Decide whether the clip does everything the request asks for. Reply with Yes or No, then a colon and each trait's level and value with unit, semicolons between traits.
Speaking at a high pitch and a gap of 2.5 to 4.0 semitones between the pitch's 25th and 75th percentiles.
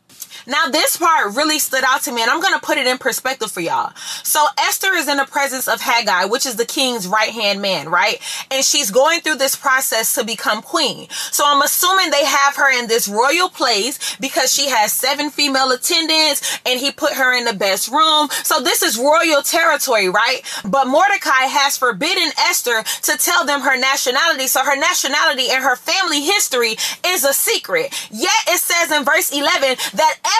Yes: very high, 280 Hz; average, 3.7 semitones